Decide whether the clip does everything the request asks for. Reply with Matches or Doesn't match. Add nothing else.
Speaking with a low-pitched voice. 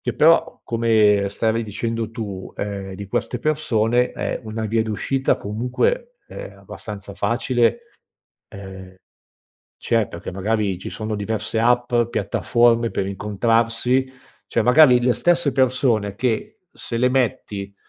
Matches